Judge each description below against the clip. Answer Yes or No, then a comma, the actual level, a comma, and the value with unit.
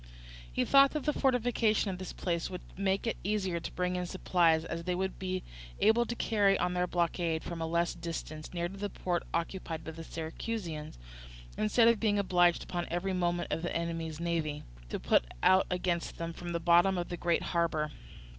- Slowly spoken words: No, average, 200 wpm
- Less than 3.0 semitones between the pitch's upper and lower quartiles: Yes, narrow, 2.5 semitones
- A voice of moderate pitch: Yes, medium, 175 Hz